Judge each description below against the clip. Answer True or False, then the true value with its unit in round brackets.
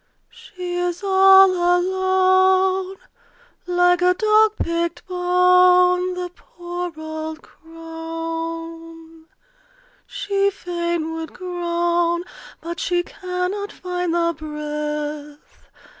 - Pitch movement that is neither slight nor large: False (1.9 semitones)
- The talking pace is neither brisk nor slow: False (85 wpm)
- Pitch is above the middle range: True (355 Hz)